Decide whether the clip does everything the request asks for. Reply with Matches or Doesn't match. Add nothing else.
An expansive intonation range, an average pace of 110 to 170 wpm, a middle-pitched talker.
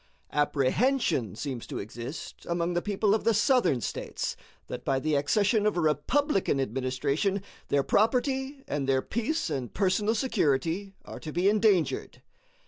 Matches